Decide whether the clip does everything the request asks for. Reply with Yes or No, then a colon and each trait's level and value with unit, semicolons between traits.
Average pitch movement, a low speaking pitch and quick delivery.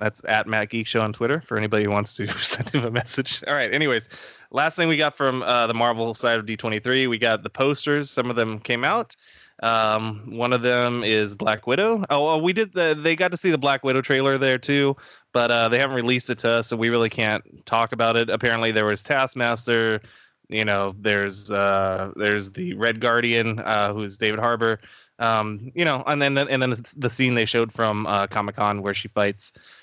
Yes: average, 3.3 semitones; low, 115 Hz; fast, 220 wpm